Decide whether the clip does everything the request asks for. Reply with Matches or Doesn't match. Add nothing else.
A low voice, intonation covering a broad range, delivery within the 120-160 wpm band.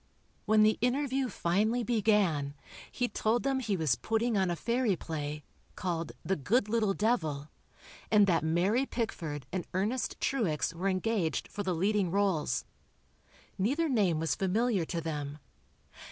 Doesn't match